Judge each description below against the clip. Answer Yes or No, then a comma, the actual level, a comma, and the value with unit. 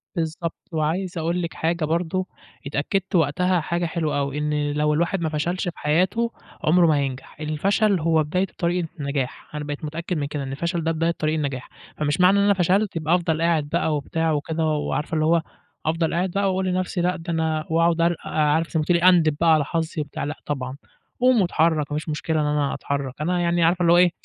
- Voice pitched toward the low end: No, medium, 165 Hz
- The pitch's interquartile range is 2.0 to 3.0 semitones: Yes, average, 2.7 semitones